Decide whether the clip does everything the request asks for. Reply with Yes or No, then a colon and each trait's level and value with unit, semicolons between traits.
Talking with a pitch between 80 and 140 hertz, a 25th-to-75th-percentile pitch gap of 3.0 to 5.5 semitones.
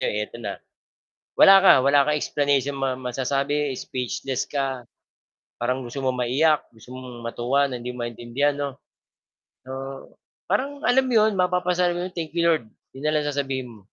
Yes: low, 135 Hz; average, 3.4 semitones